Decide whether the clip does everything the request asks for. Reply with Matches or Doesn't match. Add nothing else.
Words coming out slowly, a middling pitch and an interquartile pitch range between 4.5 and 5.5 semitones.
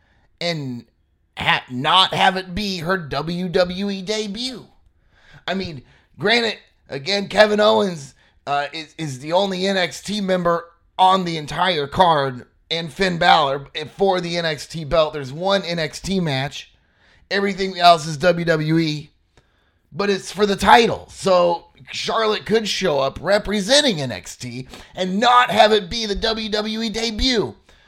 Matches